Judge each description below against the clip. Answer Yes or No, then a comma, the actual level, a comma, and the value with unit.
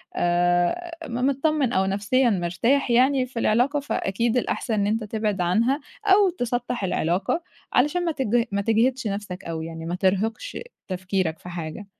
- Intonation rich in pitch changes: Yes, wide, 5.8 semitones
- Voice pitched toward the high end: Yes, high, 220 Hz